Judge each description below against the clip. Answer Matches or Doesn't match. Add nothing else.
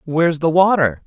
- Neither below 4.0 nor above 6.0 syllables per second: Matches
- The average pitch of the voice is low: Doesn't match